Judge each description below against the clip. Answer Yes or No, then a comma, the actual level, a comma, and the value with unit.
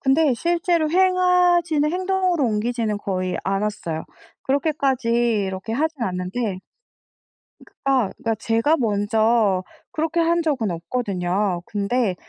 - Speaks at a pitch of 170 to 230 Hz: No, high, 240 Hz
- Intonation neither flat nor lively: No, wide, 7.7 semitones